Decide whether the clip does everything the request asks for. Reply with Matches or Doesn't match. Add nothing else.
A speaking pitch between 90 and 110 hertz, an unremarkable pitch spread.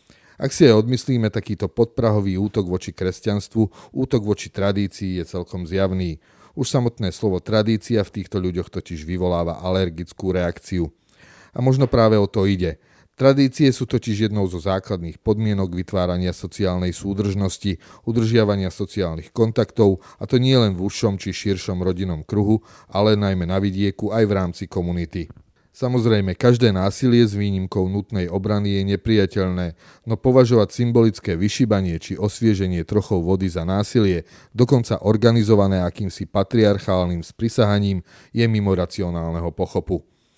Matches